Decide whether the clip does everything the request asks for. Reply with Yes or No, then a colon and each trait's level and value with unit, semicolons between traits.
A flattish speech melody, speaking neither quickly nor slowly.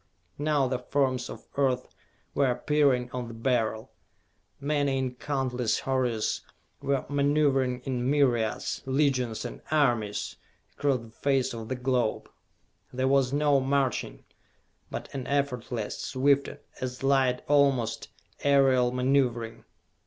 No: narrow, 2.2 semitones; slow, 120 wpm